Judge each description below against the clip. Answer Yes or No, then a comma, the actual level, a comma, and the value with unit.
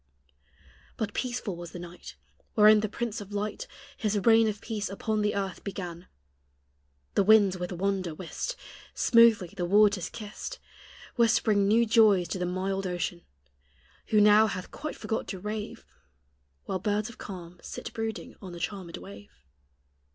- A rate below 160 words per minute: Yes, average, 150 wpm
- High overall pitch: Yes, high, 205 Hz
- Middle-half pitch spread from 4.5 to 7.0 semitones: No, average, 3.1 semitones